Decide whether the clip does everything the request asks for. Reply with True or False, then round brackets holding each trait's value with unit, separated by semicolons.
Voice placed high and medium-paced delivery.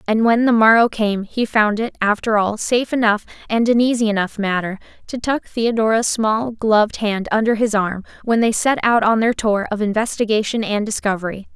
True (220 Hz; 190 wpm)